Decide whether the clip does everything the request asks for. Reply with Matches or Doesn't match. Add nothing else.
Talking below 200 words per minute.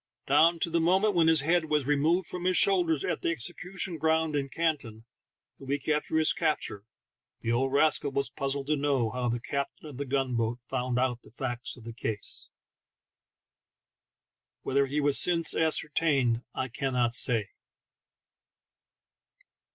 Matches